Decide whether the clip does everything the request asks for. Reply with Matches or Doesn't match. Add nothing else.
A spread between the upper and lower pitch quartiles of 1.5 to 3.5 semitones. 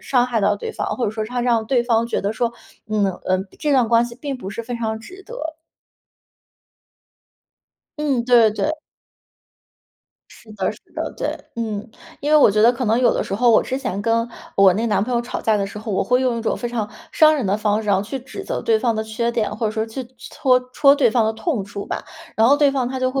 Matches